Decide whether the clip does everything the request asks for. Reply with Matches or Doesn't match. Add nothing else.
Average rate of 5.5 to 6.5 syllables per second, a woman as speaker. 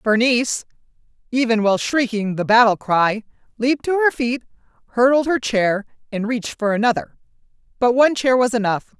Matches